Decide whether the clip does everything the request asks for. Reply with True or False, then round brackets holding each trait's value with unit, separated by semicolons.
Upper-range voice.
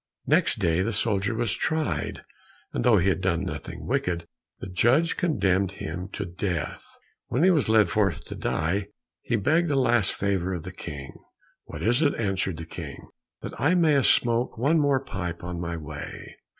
False (100 Hz)